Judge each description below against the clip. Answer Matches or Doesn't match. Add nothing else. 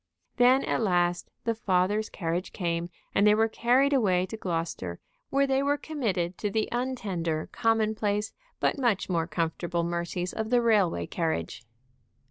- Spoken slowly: Doesn't match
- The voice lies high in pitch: Matches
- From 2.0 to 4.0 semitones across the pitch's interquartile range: Doesn't match